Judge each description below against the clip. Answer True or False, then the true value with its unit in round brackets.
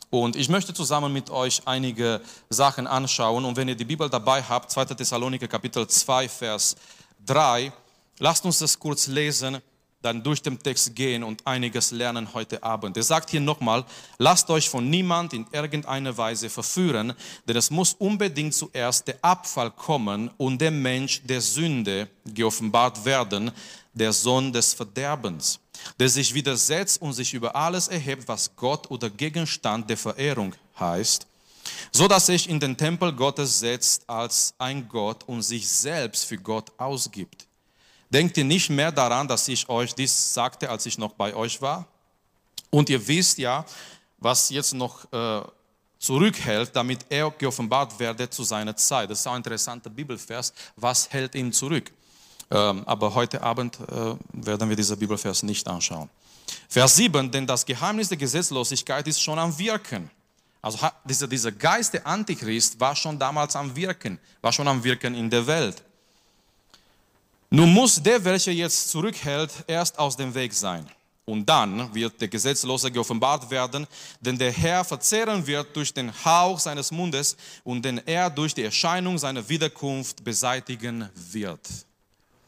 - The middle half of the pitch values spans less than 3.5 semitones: False (4.3 semitones)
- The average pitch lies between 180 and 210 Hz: False (130 Hz)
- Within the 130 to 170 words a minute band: True (160 wpm)